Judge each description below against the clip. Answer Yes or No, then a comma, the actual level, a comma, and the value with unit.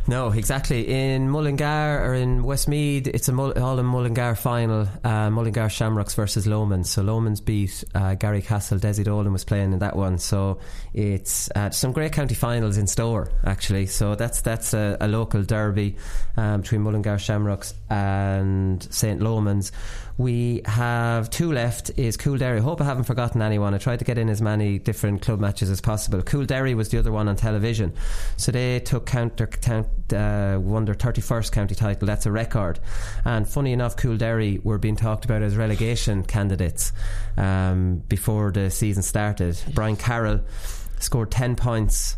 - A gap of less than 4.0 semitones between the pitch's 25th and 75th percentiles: Yes, average, 2.8 semitones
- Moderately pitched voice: No, low, 110 Hz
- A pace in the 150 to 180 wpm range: Yes, average, 175 wpm